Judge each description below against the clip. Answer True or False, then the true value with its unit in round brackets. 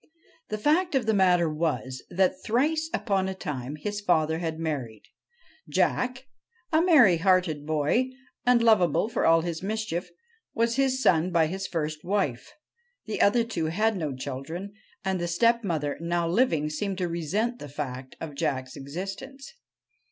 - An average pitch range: False (6.0 semitones)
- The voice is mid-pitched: True (180 Hz)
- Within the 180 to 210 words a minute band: False (155 wpm)